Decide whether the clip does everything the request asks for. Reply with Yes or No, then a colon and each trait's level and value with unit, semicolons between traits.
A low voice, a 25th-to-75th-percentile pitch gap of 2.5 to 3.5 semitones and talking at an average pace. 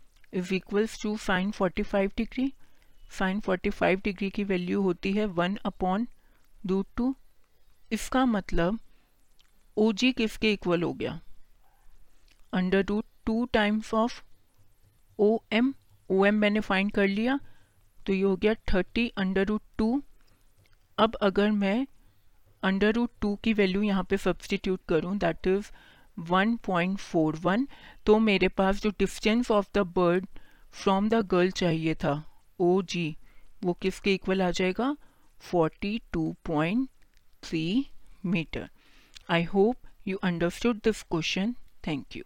No: high, 195 Hz; average, 3.2 semitones; average, 120 wpm